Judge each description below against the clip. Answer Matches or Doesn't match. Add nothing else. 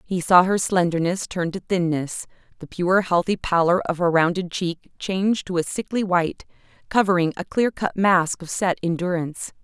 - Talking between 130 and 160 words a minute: Doesn't match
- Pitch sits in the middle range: Matches